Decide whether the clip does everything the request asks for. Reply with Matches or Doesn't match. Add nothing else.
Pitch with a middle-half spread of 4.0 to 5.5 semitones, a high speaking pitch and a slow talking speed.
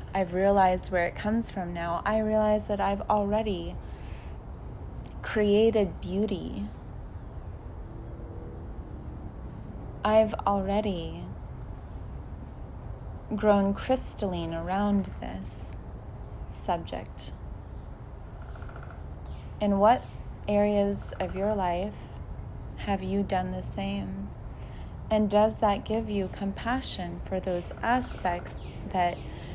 Doesn't match